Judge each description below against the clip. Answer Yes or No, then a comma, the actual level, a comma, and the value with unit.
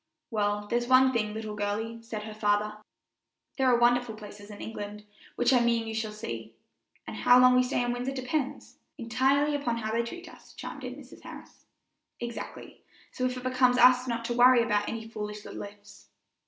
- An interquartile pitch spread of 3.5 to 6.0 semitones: No, average, 2.9 semitones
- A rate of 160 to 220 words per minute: Yes, average, 195 wpm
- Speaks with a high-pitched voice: Yes, high, 230 Hz